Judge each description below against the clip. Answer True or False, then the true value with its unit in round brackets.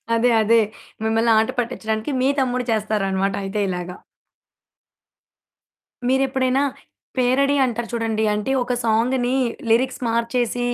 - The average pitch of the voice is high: True (230 Hz)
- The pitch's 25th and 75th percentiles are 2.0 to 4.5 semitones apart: True (2.7 semitones)